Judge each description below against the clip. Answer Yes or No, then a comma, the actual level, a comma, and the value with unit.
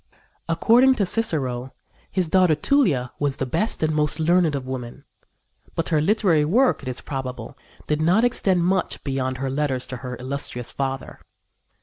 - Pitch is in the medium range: Yes, medium, 150 Hz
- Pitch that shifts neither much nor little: No, wide, 5.8 semitones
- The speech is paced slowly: No, average, 160 wpm